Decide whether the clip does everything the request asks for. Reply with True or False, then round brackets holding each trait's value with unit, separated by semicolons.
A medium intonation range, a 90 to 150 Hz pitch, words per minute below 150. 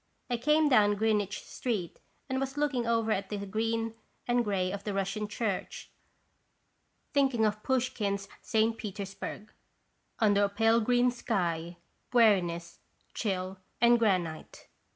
False (3.2 semitones; 215 Hz; 135 wpm)